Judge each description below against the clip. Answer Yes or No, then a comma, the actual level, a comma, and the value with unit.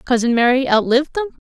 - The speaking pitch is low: No, very high, 260 Hz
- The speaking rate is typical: Yes, average, 160 wpm